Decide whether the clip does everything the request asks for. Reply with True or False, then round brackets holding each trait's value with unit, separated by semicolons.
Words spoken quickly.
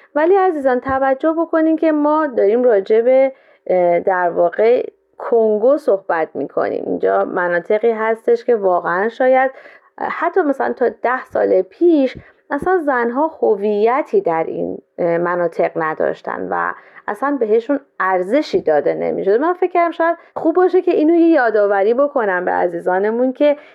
False (135 wpm)